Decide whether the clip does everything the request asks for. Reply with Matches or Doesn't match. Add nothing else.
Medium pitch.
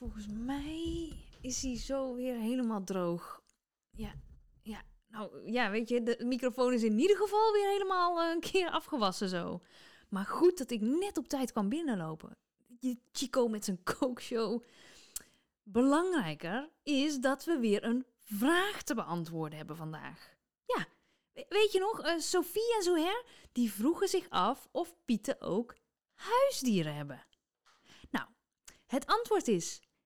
Doesn't match